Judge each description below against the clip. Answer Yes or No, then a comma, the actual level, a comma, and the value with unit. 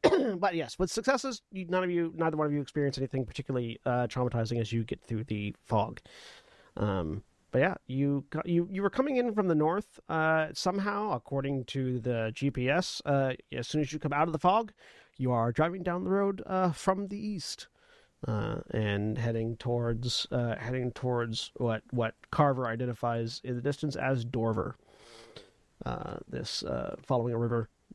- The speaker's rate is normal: Yes, average, 175 wpm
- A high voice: No, low, 135 Hz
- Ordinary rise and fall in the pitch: No, wide, 6.7 semitones